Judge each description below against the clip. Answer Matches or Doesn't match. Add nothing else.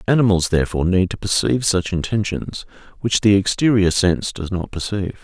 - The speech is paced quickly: Doesn't match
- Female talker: Doesn't match